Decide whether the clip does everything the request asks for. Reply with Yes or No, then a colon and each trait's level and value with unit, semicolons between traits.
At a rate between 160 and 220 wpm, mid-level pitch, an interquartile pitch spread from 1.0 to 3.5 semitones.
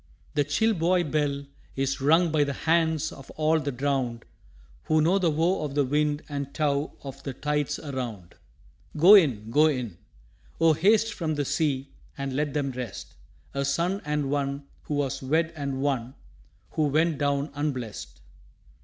Yes: average, 165 wpm; medium, 145 Hz; narrow, 2.5 semitones